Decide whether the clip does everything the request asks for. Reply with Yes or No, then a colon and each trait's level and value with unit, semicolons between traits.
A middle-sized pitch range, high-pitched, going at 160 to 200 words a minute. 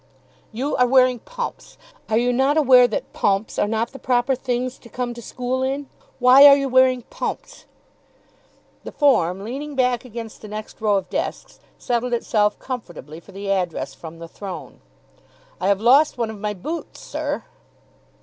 Yes: average, 3.8 semitones; high, 245 Hz; average, 170 wpm